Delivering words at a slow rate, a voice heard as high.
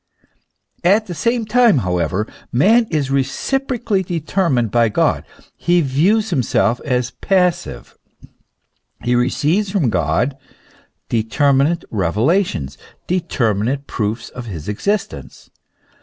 No: slow, 110 wpm; medium, 140 Hz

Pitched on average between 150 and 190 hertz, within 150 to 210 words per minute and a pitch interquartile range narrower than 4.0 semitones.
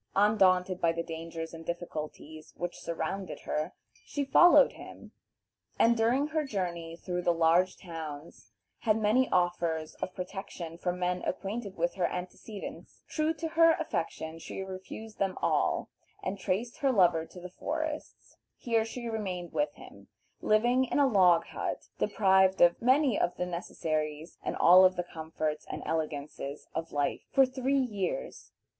No: medium, 185 Hz; average, 155 wpm; average, 5.3 semitones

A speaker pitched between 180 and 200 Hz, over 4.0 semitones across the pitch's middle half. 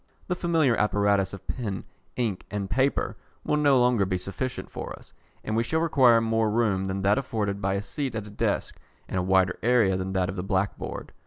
No: low, 105 Hz; average, 4.4 semitones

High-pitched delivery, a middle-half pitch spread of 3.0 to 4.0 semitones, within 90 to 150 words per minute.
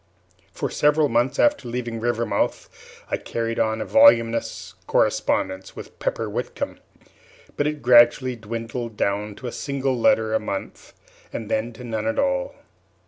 No: low, 120 Hz; average, 3.5 semitones; average, 145 wpm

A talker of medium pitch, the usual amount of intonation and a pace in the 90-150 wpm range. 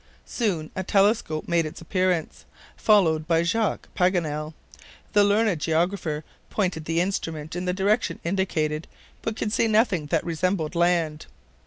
Yes: medium, 175 Hz; average, 4.0 semitones; average, 140 wpm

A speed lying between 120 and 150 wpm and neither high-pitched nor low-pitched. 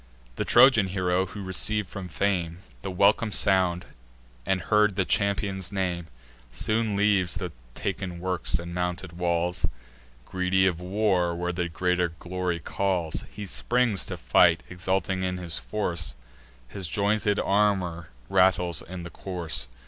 No: slow, 135 wpm; very low, 90 Hz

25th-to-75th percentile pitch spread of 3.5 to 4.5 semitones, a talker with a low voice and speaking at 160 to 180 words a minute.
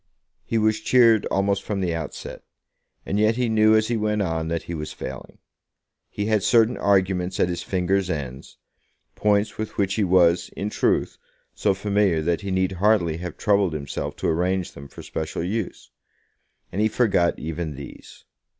Yes: average, 3.8 semitones; very low, 95 Hz; average, 175 wpm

